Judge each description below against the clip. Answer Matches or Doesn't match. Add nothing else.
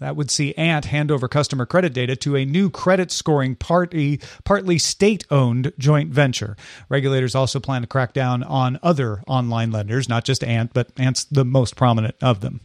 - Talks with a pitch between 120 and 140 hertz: Matches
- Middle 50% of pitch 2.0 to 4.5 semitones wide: Matches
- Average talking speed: Matches